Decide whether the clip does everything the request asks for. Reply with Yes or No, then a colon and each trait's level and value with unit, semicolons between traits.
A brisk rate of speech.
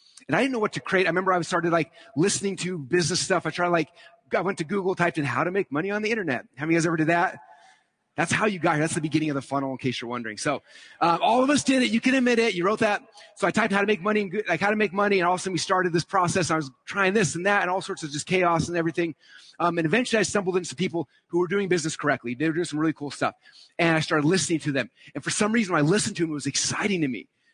Yes: fast, 310 wpm